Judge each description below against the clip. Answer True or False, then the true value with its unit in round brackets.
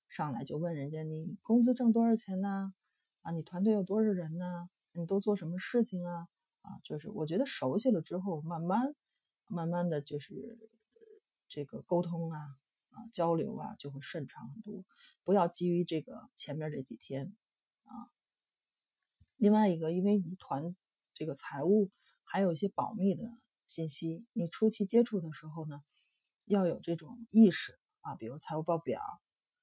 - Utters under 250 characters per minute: True (240 characters per minute)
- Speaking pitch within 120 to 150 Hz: False (180 Hz)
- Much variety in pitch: False (4.5 semitones)